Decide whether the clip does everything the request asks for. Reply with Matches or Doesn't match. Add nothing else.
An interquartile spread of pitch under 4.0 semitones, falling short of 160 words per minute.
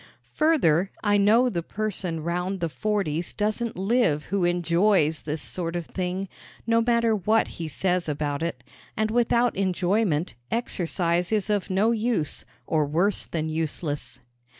Doesn't match